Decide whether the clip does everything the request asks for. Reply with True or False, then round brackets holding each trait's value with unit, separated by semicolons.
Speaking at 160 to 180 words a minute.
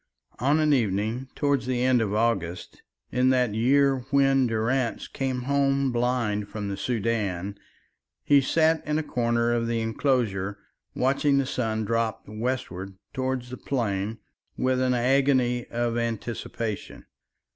False (135 wpm)